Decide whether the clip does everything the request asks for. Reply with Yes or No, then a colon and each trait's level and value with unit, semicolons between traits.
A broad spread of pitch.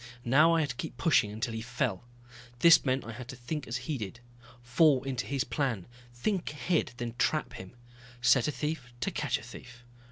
No: average, 3.9 semitones